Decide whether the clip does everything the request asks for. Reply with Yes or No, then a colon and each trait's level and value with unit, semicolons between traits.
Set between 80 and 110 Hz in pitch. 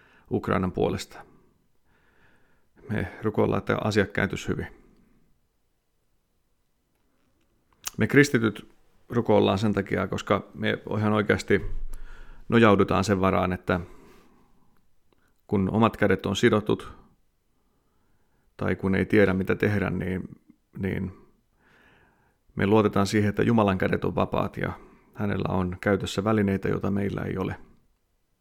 Yes: low, 100 Hz